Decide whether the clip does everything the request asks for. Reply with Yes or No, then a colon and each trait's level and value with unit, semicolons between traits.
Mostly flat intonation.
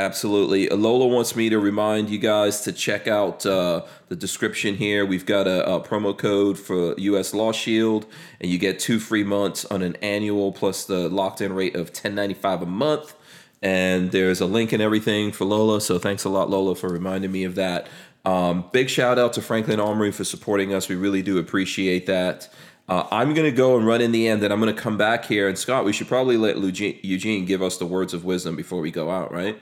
Yes: narrow, 2.3 semitones